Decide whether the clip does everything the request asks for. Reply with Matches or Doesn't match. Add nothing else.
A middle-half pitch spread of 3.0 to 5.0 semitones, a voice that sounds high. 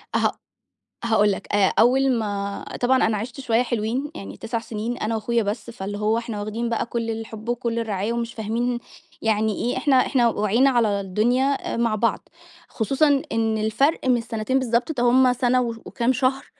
Doesn't match